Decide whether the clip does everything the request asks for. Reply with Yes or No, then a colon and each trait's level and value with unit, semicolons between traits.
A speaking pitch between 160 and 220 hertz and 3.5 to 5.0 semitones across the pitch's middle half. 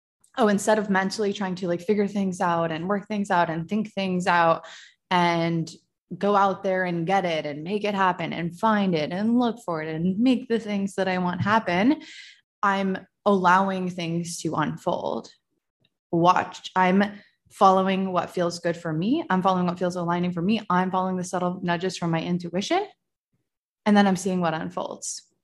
No: medium, 185 Hz; average, 2.8 semitones